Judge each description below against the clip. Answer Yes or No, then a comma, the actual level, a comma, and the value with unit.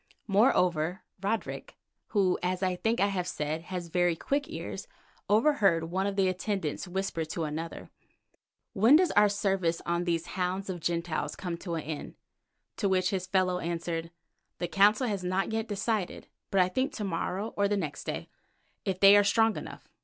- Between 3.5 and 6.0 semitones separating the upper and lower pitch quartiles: No, average, 2.9 semitones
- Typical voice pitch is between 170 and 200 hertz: Yes, medium, 185 Hz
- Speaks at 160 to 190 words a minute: Yes, average, 175 wpm